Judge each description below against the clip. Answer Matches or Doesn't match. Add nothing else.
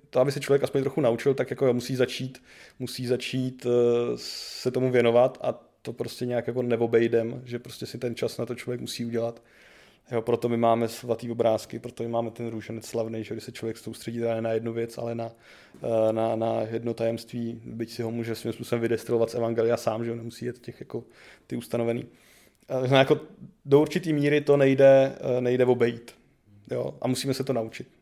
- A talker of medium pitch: Doesn't match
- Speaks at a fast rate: Matches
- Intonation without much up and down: Matches